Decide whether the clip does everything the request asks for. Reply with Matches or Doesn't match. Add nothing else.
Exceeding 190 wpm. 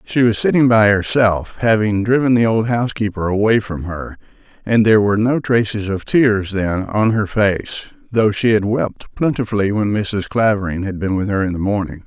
Matches